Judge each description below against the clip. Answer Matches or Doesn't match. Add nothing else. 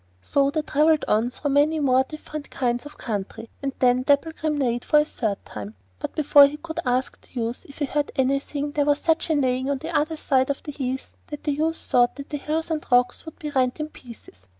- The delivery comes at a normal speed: Doesn't match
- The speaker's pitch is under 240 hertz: Doesn't match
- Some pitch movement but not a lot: Matches